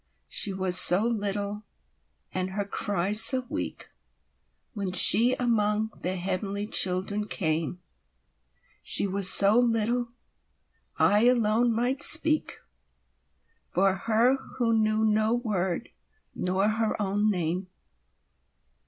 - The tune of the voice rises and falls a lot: No, average, 3.3 semitones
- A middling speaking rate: No, slow, 95 wpm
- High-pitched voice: Yes, high, 205 Hz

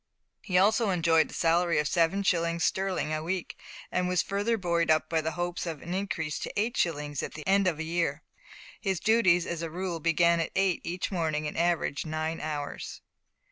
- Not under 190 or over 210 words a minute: Yes, average, 200 wpm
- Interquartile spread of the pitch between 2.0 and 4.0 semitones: Yes, narrow, 2.6 semitones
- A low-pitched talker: No, medium, 170 Hz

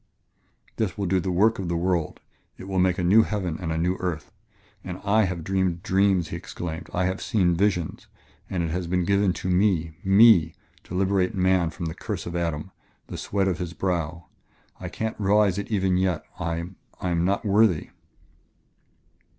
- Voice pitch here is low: Yes, very low, 90 Hz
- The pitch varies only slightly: Yes, narrow, 2.2 semitones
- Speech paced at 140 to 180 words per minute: No, average, 190 wpm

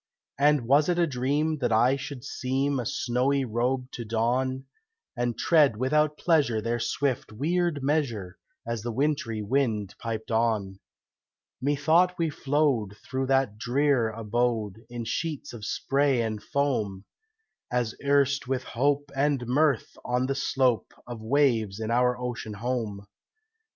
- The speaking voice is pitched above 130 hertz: No, low, 125 Hz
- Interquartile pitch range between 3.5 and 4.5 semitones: Yes, average, 3.8 semitones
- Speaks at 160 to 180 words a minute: No, average, 140 wpm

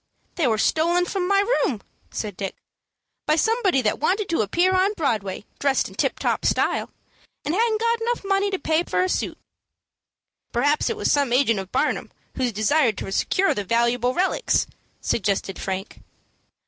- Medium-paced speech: Yes, average, 170 wpm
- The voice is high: Yes, very high, 300 Hz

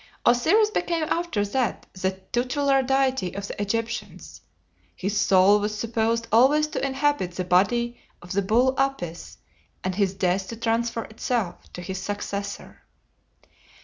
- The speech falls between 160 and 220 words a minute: No, average, 145 wpm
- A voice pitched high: Yes, high, 225 Hz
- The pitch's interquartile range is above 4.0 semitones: Yes, average, 5.1 semitones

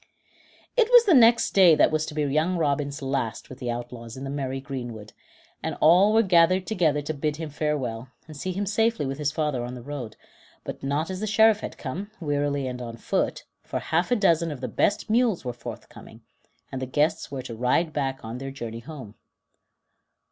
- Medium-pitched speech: Yes, medium, 145 Hz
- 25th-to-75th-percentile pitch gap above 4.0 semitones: Yes, wide, 5.6 semitones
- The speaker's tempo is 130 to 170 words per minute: No, fast, 205 wpm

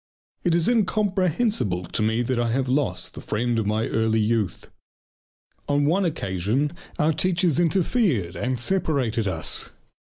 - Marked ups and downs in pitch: Yes, wide, 7.8 semitones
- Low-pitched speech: Yes, low, 130 Hz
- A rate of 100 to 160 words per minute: Yes, average, 140 wpm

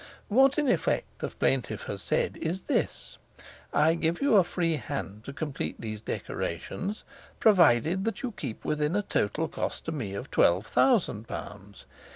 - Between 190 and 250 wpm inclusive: No, average, 165 wpm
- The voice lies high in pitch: No, medium, 160 Hz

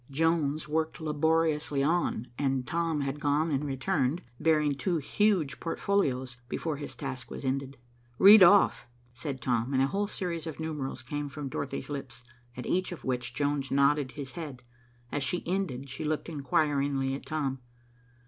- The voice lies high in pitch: No, medium, 145 Hz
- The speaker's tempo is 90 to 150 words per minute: No, average, 160 wpm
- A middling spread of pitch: Yes, average, 3.1 semitones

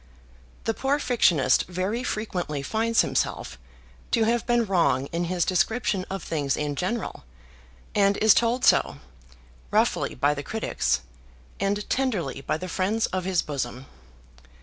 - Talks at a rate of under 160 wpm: Yes, average, 140 wpm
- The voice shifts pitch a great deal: Yes, wide, 6.6 semitones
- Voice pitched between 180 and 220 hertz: Yes, high, 190 Hz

